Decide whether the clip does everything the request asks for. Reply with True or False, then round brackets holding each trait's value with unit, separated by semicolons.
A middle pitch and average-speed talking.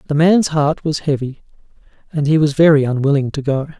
True (150 Hz; 190 wpm)